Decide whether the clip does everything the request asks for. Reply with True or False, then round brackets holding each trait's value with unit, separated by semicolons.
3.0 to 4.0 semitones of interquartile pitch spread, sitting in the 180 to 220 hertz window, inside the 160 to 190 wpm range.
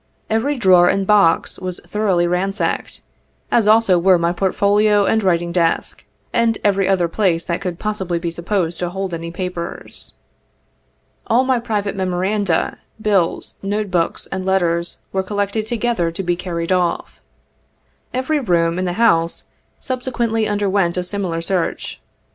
False (3.4 semitones; 190 Hz; 150 wpm)